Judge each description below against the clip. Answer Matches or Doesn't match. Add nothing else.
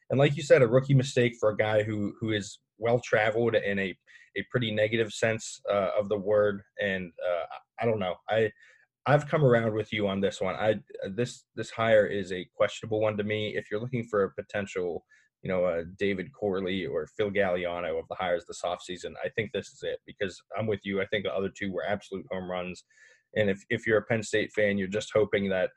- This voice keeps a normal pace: Doesn't match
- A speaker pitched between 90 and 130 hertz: Matches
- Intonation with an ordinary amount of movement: Matches